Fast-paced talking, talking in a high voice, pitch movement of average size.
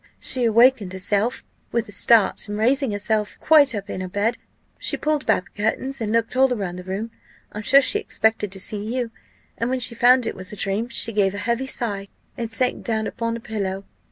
Yes: fast, 215 wpm; high, 225 Hz; average, 3.3 semitones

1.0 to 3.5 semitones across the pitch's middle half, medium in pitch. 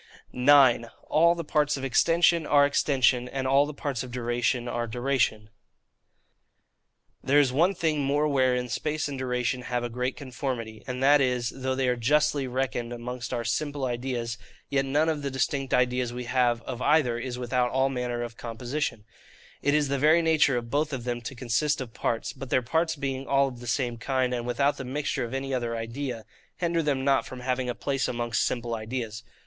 No: average, 2.7 semitones; low, 130 Hz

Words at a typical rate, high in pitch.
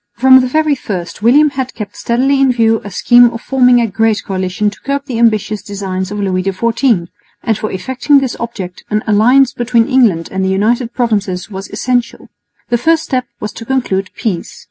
Yes: average, 190 wpm; high, 230 Hz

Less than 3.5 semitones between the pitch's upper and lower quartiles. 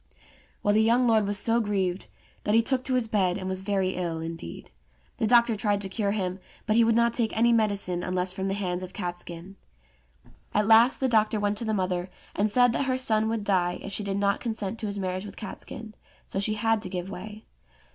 Yes: average, 3.1 semitones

